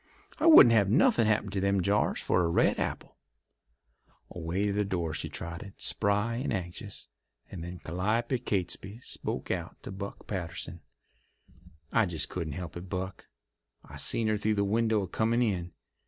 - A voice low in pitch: Yes, low, 100 Hz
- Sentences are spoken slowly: No, average, 170 wpm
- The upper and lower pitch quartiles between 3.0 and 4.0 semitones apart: Yes, average, 3.6 semitones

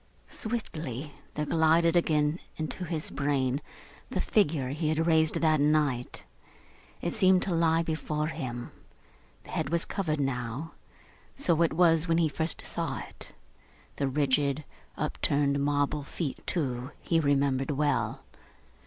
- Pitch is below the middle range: No, medium, 150 Hz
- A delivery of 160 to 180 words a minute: No, slow, 135 wpm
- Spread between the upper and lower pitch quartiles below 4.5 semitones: Yes, average, 2.8 semitones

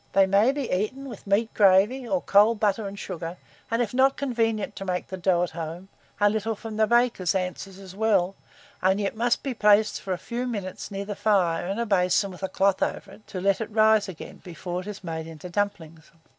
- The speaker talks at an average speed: No, fast, 225 wpm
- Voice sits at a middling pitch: No, high, 200 Hz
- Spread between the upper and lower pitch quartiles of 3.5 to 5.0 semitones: No, average, 3.0 semitones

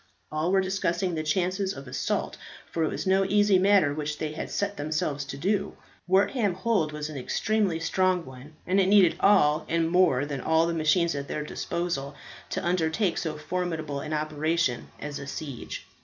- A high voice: No, medium, 165 Hz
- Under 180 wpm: No, average, 185 wpm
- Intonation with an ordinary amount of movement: Yes, average, 3.7 semitones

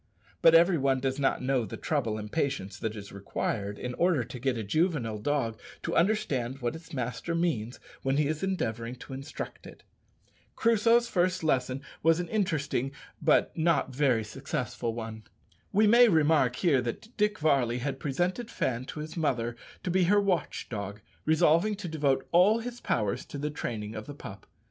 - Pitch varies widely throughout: Yes, wide, 6.2 semitones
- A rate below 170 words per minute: No, average, 180 wpm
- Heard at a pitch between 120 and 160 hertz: Yes, medium, 140 Hz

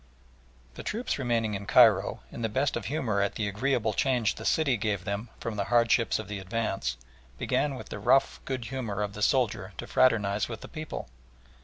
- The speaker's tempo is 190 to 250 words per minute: Yes, average, 195 wpm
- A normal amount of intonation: Yes, average, 4.0 semitones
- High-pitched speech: No, low, 115 Hz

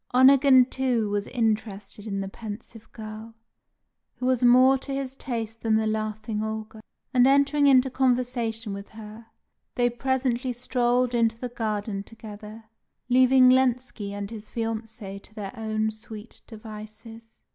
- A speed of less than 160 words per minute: Yes, average, 140 wpm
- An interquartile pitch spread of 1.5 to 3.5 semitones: Yes, average, 2.7 semitones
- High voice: Yes, high, 225 Hz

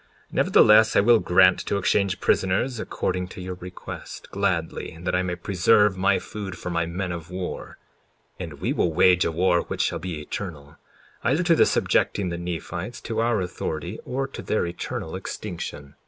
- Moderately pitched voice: No, very low, 90 Hz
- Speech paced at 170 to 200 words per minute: Yes, average, 180 wpm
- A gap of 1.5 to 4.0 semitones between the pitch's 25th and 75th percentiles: Yes, average, 3.0 semitones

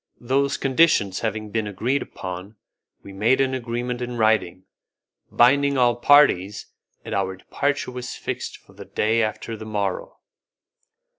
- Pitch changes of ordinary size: Yes, average, 4.1 semitones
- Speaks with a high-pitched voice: No, low, 115 Hz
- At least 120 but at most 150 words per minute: Yes, average, 145 wpm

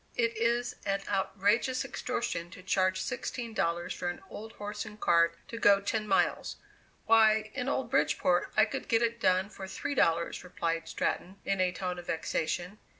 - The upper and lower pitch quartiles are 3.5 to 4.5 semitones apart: Yes, average, 4.1 semitones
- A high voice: Yes, high, 200 Hz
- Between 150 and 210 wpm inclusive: Yes, average, 175 wpm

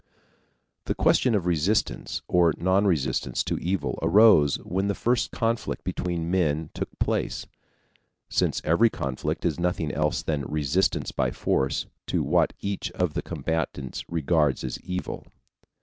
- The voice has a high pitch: No, very low, 85 Hz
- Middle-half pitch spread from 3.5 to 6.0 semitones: Yes, average, 4.2 semitones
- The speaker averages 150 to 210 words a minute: No, average, 140 wpm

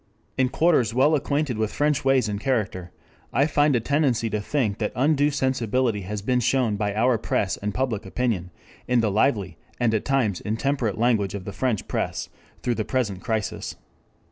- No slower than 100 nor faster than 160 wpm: No, average, 180 wpm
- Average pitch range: Yes, average, 4.3 semitones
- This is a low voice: Yes, low, 115 Hz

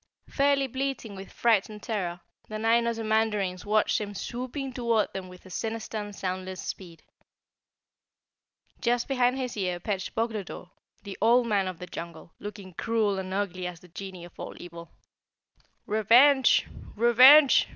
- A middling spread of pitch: Yes, average, 4.0 semitones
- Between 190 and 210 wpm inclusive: No, average, 150 wpm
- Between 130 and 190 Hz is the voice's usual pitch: No, high, 210 Hz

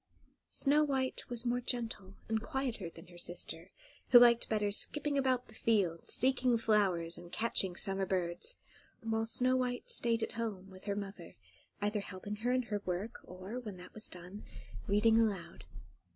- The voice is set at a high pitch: Yes, high, 220 Hz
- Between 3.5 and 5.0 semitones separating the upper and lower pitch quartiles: Yes, average, 4.3 semitones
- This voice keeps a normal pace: Yes, average, 165 wpm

